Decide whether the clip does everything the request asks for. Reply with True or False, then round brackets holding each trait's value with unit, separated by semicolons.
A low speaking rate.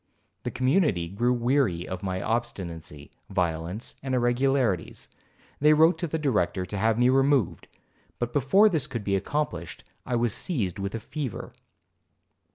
False (150 wpm)